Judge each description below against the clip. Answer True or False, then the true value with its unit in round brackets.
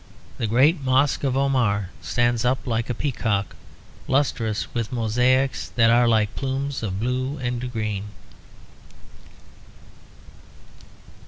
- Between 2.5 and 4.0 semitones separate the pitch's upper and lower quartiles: True (2.9 semitones)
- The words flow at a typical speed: False (110 wpm)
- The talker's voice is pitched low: True (125 Hz)